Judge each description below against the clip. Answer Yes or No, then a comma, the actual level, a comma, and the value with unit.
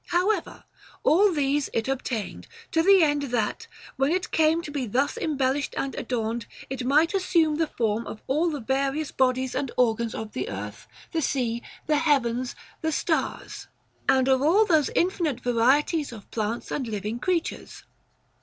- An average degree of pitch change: Yes, average, 5.0 semitones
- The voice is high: Yes, very high, 270 Hz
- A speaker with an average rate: Yes, average, 165 wpm